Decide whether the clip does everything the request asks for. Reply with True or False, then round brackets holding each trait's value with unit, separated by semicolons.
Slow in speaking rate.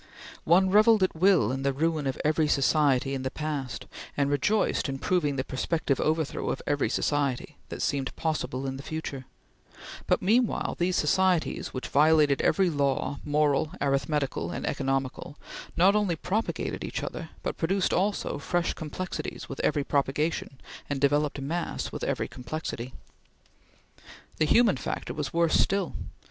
False (150 wpm)